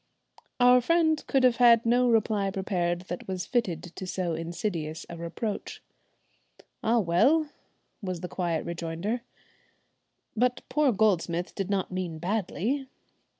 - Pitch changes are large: Yes, wide, 5.7 semitones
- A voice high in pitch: Yes, high, 195 Hz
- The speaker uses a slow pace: Yes, slow, 130 wpm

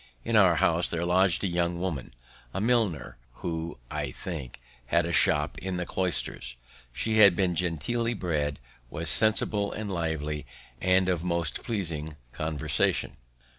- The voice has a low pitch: Yes, very low, 85 Hz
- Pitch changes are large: No, average, 3.5 semitones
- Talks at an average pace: Yes, average, 145 wpm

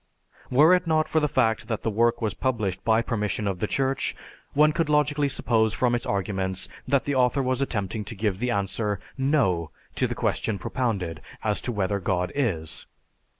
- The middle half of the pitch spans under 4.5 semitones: No, average, 5.2 semitones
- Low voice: Yes, low, 115 Hz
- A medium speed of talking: Yes, average, 190 wpm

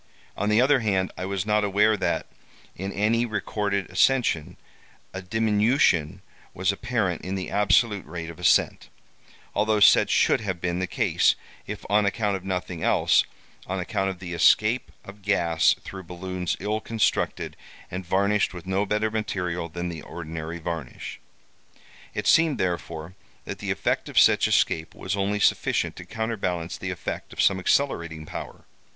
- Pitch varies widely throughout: No, average, 3.2 semitones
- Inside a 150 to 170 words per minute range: Yes, average, 160 wpm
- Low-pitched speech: Yes, very low, 95 Hz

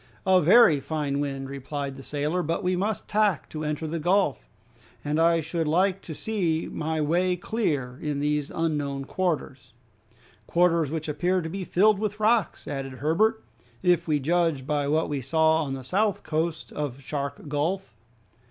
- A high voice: No, medium, 160 Hz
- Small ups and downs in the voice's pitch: No, average, 3.8 semitones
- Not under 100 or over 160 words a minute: No, average, 170 wpm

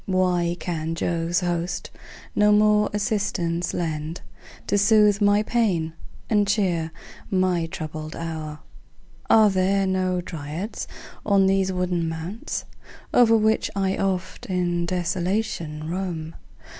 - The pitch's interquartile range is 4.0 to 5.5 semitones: No, average, 3.3 semitones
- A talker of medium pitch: Yes, medium, 180 Hz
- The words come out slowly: Yes, slow, 115 wpm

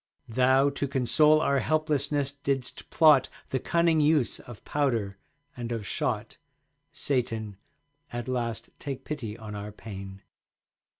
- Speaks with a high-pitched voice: No, low, 130 Hz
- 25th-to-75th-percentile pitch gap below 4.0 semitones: No, average, 4.3 semitones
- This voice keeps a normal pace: No, slow, 125 wpm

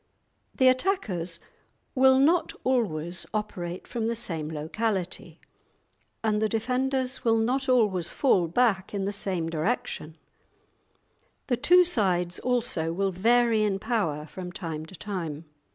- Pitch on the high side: Yes, high, 210 Hz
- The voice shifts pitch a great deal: Yes, wide, 6.0 semitones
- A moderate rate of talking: No, slow, 130 wpm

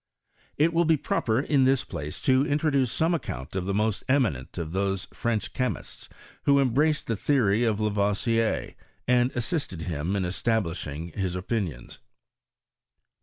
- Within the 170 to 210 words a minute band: No, average, 150 wpm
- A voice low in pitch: Yes, low, 110 Hz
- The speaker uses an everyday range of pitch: No, wide, 6.3 semitones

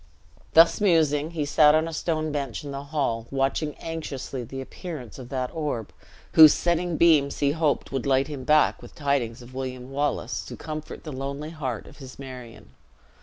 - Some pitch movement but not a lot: Yes, average, 3.0 semitones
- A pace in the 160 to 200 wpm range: Yes, average, 180 wpm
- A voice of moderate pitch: Yes, medium, 145 Hz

